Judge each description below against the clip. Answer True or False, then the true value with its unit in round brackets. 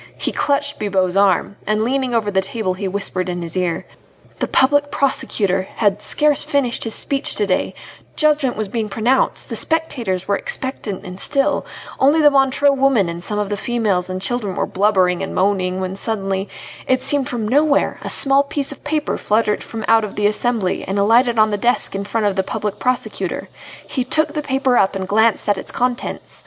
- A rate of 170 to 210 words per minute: True (195 wpm)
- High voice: True (220 Hz)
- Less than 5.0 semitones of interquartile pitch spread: False (5.4 semitones)